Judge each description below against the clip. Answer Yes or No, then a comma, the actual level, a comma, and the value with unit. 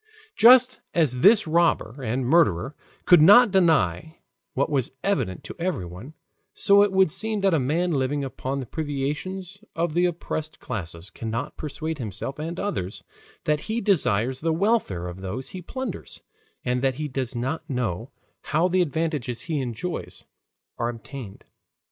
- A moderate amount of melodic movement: No, wide, 6.2 semitones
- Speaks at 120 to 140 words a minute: No, average, 155 wpm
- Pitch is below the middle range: No, medium, 150 Hz